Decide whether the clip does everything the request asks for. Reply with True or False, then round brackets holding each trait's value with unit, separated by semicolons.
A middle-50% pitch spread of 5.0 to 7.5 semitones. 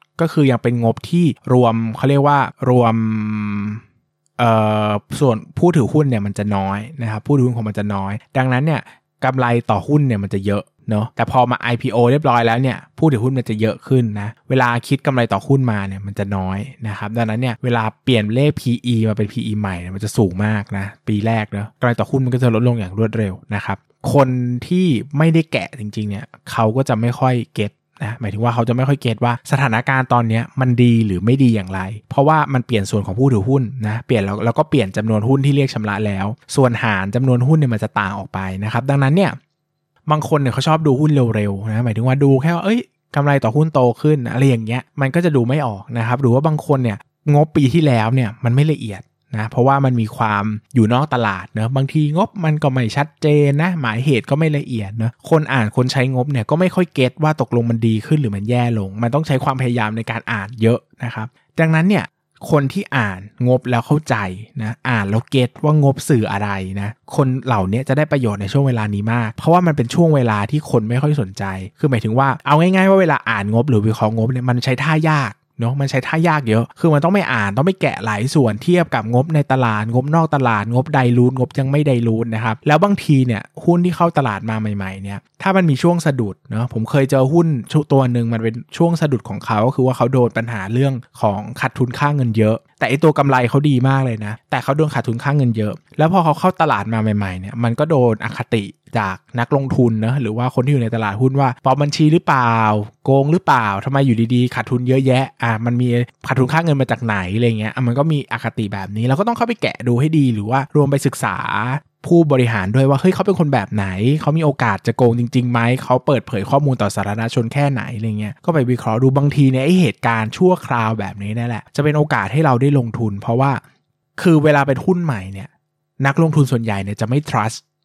False (4.3 semitones)